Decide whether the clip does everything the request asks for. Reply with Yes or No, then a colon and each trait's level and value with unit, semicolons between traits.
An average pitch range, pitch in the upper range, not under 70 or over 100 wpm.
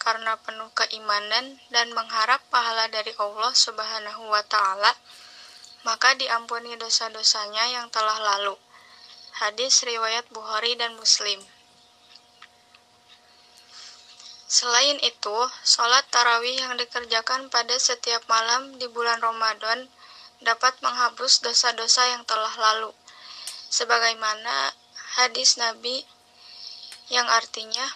No: narrow, 1.9 semitones; high, 230 Hz; average, 95 wpm